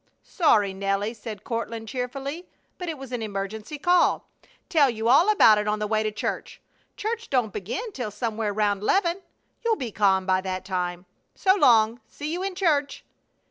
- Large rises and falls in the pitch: Yes, wide, 6.9 semitones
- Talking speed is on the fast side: No, average, 175 wpm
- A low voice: No, high, 230 Hz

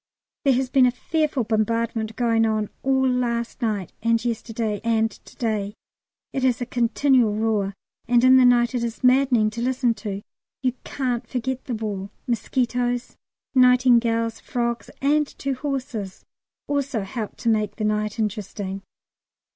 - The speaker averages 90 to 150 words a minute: Yes, average, 145 wpm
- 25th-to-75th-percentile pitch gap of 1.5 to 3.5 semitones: Yes, narrow, 2.6 semitones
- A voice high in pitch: Yes, high, 235 Hz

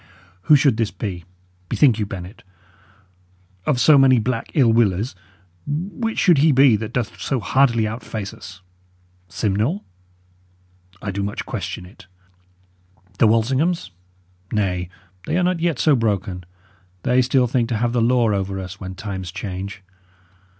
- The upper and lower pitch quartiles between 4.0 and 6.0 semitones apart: Yes, average, 5.1 semitones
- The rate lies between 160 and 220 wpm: No, average, 145 wpm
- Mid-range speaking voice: No, low, 115 Hz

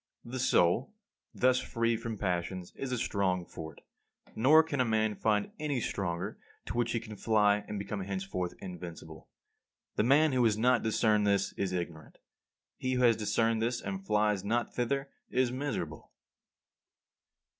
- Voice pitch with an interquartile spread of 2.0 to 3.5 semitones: No, average, 4.5 semitones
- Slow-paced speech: No, average, 155 wpm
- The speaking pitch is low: Yes, low, 110 Hz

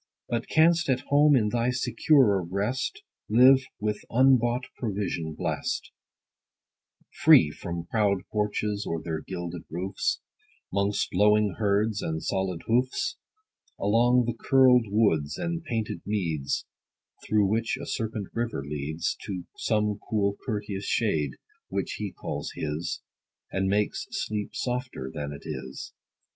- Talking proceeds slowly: Yes, slow, 130 wpm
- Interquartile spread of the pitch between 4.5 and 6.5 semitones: Yes, average, 4.8 semitones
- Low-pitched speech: Yes, low, 105 Hz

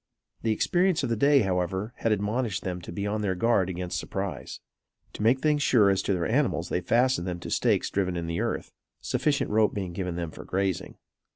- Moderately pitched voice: No, low, 100 Hz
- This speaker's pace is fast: Yes, fast, 210 wpm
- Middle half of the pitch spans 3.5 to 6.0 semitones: Yes, average, 4.4 semitones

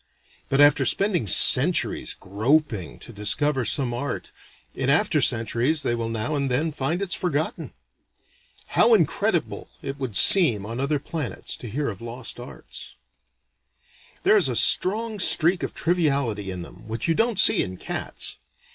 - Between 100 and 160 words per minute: Yes, average, 155 wpm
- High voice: No, low, 135 Hz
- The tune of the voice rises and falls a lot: Yes, wide, 5.8 semitones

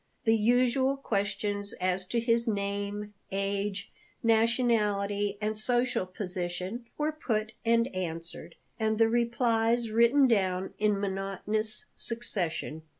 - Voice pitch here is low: No, high, 215 Hz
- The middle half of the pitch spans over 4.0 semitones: No, average, 2.9 semitones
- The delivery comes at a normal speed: No, slow, 110 wpm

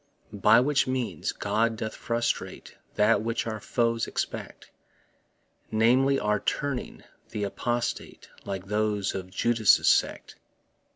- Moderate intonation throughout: No, narrow, 2.3 semitones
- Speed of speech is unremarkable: No, slow, 115 wpm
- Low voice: Yes, low, 115 Hz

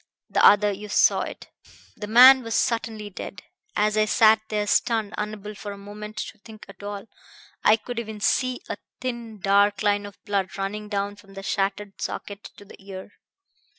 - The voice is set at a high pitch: Yes, high, 210 Hz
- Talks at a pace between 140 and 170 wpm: No, average, 185 wpm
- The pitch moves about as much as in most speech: No, narrow, 1.3 semitones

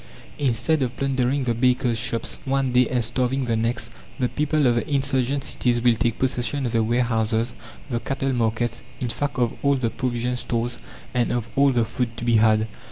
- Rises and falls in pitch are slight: Yes, narrow, 2.2 semitones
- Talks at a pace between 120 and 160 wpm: No, average, 195 wpm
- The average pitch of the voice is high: No, low, 120 Hz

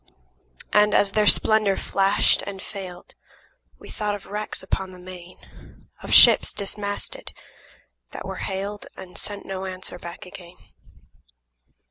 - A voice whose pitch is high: Yes, high, 195 Hz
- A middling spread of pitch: No, narrow, 1.9 semitones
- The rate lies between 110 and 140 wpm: Yes, slow, 135 wpm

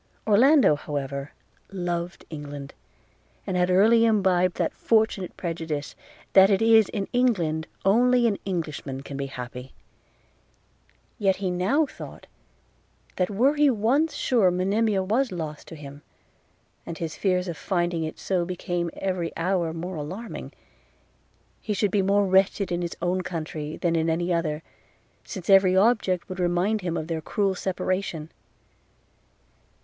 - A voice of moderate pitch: Yes, medium, 180 Hz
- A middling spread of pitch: Yes, average, 3.7 semitones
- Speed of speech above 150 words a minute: No, average, 145 wpm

